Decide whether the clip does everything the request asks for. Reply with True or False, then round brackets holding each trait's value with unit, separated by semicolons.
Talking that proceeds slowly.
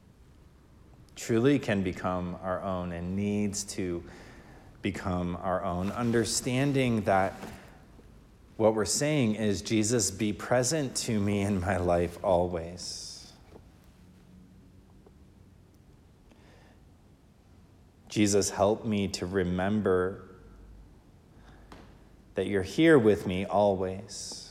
True (90 wpm)